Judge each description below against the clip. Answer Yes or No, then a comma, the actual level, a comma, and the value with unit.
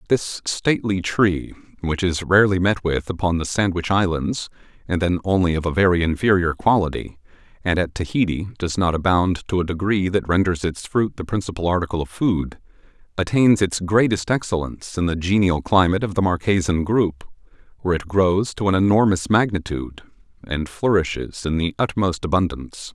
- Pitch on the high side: No, very low, 90 Hz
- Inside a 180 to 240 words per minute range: No, average, 165 wpm